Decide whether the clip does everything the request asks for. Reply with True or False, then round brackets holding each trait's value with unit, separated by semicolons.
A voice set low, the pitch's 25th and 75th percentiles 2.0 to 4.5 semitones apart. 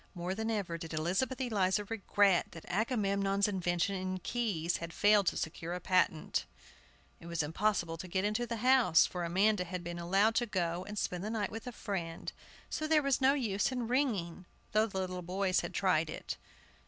False (195 Hz; 4.0 semitones)